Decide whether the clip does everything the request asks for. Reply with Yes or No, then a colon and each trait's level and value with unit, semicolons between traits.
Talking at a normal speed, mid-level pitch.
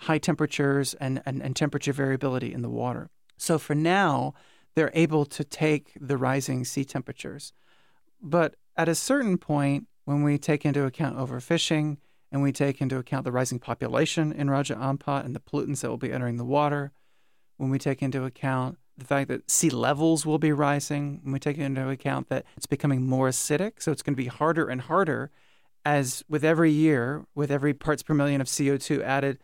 Yes: average, 195 wpm; medium, 145 Hz